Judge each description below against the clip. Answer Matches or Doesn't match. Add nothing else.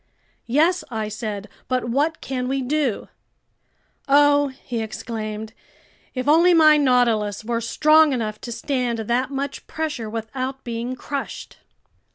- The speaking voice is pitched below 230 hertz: Doesn't match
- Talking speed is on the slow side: Matches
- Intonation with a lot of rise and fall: Doesn't match